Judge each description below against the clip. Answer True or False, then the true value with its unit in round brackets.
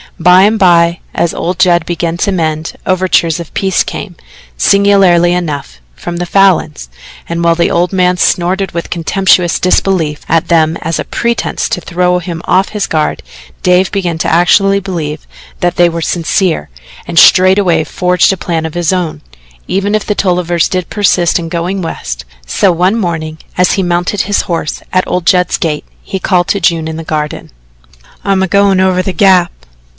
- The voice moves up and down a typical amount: False (2.1 semitones)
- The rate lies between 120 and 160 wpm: False (180 wpm)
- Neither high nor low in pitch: True (175 Hz)